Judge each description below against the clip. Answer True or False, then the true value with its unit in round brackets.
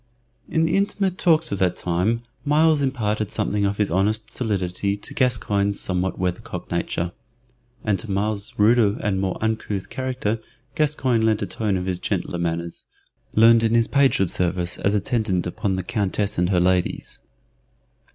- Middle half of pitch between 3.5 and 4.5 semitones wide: True (3.9 semitones)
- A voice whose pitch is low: True (105 Hz)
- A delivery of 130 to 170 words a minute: True (160 wpm)